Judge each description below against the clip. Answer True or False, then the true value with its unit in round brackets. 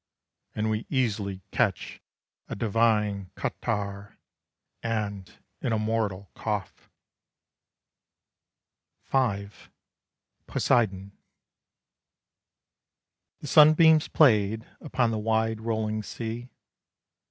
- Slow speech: True (75 wpm)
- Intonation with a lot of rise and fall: False (2.4 semitones)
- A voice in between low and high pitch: False (110 Hz)